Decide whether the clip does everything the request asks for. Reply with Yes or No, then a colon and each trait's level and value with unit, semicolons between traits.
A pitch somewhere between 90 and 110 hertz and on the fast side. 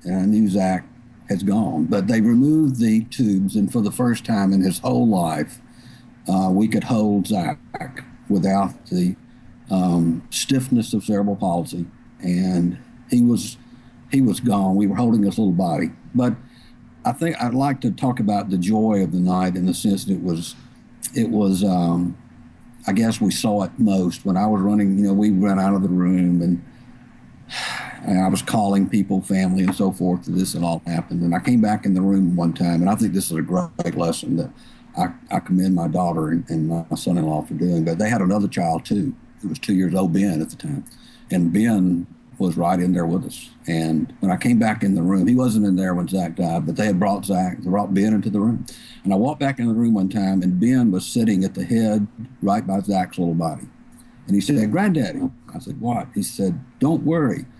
Yes: very low, 95 Hz; fast, 220 wpm